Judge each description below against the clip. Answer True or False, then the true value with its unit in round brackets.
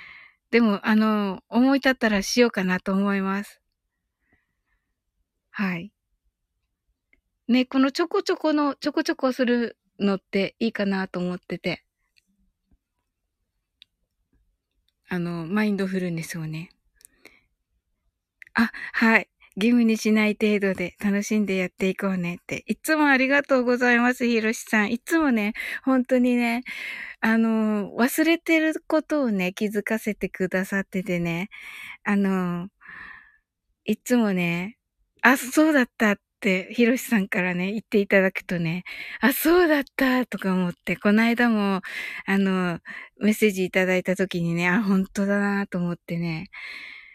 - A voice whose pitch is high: True (210 Hz)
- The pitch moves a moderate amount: True (4.7 semitones)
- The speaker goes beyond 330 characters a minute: False (270 characters per minute)